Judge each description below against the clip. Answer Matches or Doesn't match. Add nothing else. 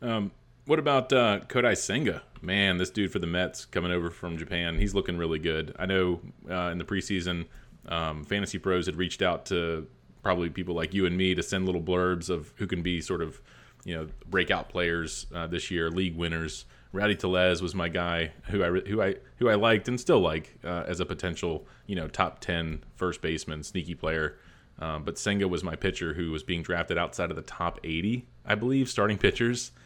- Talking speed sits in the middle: Doesn't match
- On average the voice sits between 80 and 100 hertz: Matches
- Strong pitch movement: Doesn't match